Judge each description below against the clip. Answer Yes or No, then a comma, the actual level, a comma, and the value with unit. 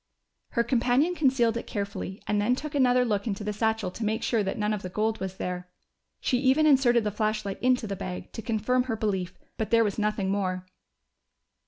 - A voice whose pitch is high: Yes, high, 220 Hz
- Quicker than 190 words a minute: Yes, fast, 205 wpm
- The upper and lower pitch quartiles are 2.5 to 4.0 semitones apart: Yes, average, 3.5 semitones